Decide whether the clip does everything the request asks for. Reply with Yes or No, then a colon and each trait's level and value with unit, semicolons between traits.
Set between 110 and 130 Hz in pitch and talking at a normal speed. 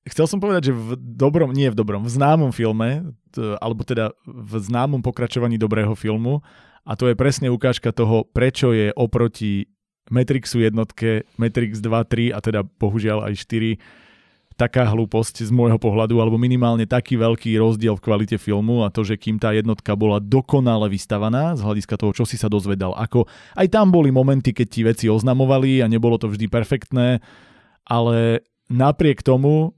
No: low, 115 Hz; fast, 170 wpm